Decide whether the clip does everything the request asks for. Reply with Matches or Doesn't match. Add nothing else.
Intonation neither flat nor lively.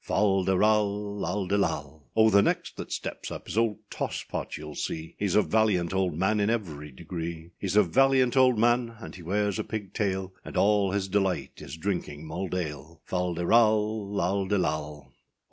Matches